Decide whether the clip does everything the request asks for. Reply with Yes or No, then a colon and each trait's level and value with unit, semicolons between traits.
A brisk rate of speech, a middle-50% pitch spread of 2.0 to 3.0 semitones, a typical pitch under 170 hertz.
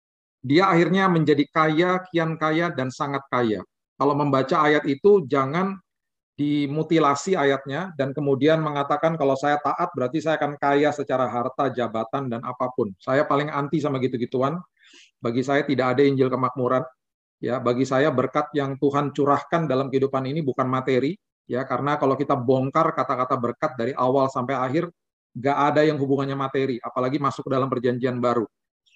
Yes: fast, 155 wpm; average, 2.7 semitones; medium, 140 Hz